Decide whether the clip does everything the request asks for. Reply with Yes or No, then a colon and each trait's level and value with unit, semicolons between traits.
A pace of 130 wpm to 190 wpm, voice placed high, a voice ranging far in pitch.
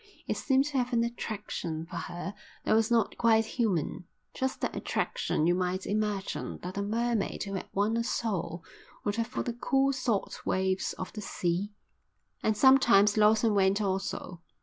No: average, 170 wpm; high, 210 Hz; average, 3.6 semitones